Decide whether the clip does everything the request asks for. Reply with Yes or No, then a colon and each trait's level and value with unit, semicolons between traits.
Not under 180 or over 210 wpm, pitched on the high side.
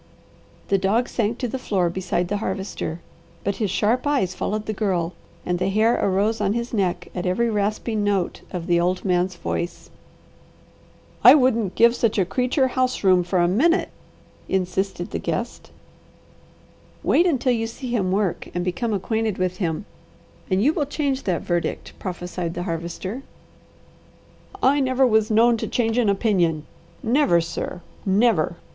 No: average, 160 wpm; high, 200 Hz